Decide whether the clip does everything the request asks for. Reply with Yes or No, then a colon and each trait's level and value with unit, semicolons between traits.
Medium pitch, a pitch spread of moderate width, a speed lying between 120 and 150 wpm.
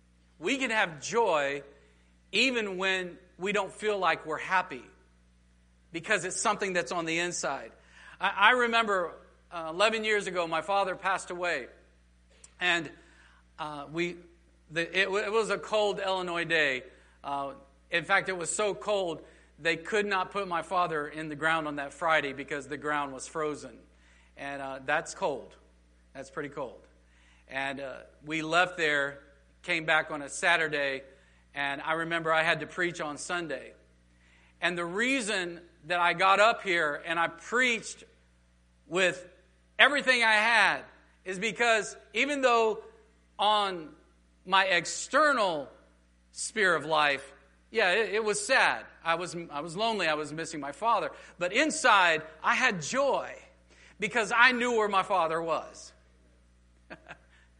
No: medium, 170 Hz; wide, 6.3 semitones; average, 140 wpm